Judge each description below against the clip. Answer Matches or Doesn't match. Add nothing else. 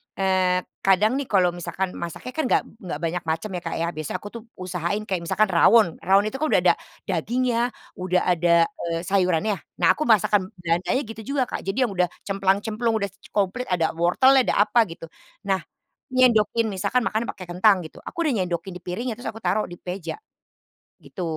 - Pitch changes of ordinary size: Matches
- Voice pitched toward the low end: Doesn't match